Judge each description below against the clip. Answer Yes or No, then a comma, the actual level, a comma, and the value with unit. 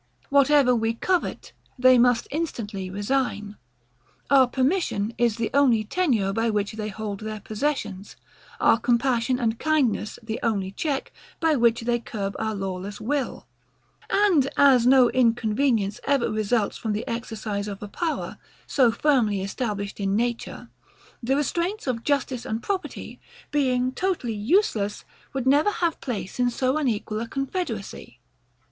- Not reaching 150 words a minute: Yes, average, 140 wpm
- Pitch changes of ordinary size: Yes, average, 4.4 semitones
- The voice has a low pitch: No, high, 235 Hz